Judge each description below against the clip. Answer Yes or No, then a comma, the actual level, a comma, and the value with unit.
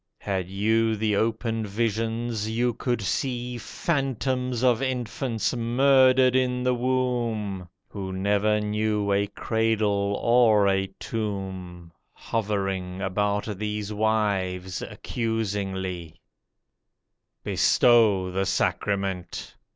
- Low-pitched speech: Yes, low, 110 Hz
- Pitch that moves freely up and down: No, average, 3.4 semitones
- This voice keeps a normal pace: No, slow, 95 wpm